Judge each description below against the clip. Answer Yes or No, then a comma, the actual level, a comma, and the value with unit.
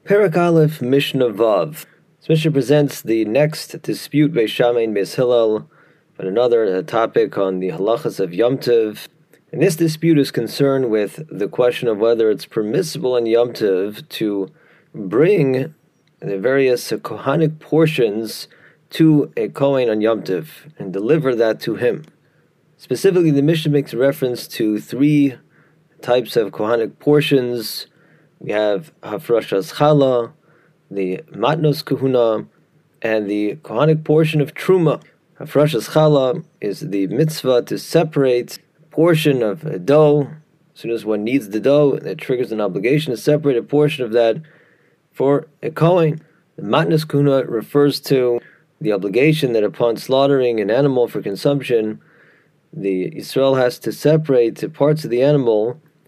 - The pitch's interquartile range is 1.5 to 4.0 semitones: No, average, 4.7 semitones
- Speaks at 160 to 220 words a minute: No, average, 140 wpm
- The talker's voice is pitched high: No, medium, 140 Hz